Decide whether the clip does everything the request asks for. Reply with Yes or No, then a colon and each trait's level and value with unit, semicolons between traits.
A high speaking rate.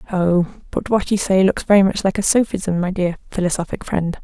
Yes: fast, 210 wpm